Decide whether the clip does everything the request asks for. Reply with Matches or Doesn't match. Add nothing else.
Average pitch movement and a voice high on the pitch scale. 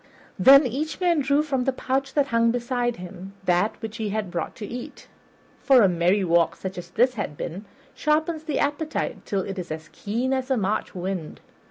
Doesn't match